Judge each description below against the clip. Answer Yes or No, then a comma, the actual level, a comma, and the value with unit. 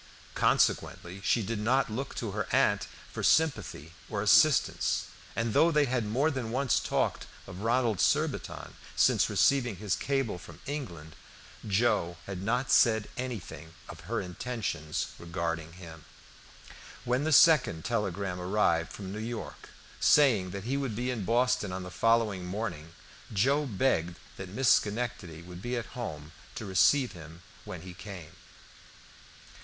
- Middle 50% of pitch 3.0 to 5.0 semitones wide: No, wide, 5.6 semitones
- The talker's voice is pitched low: Yes, low, 105 Hz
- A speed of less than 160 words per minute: Yes, average, 150 wpm